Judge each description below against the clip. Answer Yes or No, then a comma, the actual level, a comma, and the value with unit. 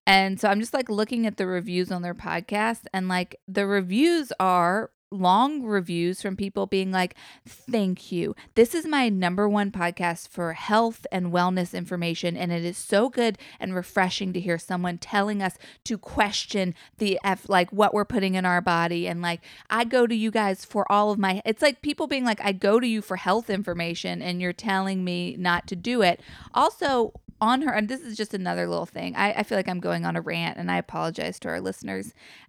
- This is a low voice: No, high, 195 Hz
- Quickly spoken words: Yes, fast, 210 wpm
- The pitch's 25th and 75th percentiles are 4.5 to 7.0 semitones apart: No, average, 3.3 semitones